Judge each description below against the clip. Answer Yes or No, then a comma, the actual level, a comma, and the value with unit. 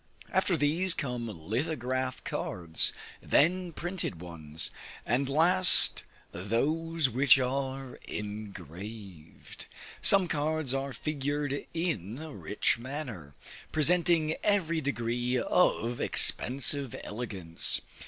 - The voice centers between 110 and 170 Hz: Yes, low, 135 Hz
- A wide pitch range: Yes, wide, 6.1 semitones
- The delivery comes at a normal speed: No, slow, 95 wpm